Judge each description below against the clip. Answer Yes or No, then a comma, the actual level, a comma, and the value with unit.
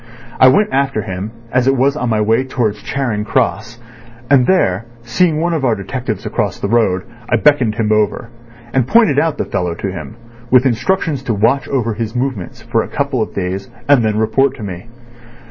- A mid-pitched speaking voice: No, low, 120 Hz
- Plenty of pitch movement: No, average, 4.2 semitones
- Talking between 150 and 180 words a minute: No, average, 195 wpm